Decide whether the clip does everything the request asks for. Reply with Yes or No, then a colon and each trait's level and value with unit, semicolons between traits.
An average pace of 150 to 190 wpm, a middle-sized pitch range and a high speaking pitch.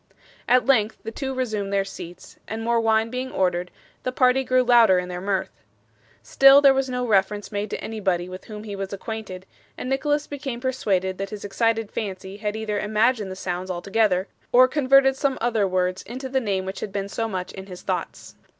No: average, 200 wpm; average, 4.7 semitones; high, 215 Hz